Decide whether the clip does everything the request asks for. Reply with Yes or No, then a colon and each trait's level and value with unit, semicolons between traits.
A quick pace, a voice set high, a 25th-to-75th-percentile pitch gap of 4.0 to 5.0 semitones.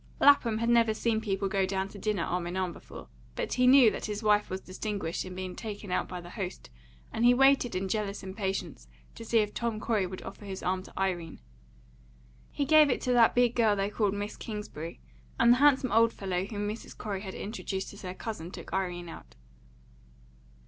No: fast, 210 wpm; high, 205 Hz; average, 3.4 semitones